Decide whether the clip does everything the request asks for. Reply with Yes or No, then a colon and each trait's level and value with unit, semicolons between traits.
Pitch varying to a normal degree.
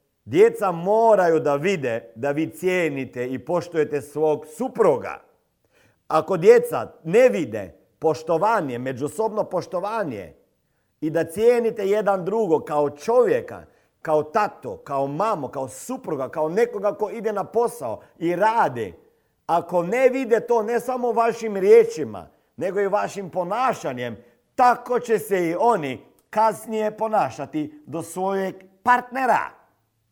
No: wide, 7.0 semitones